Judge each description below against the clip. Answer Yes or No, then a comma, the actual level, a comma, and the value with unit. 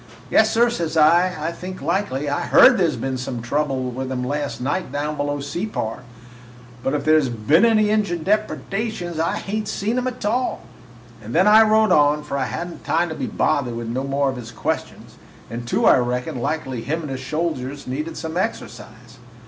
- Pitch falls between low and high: Yes, medium, 150 Hz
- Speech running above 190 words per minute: Yes, average, 200 wpm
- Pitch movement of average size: No, wide, 6.1 semitones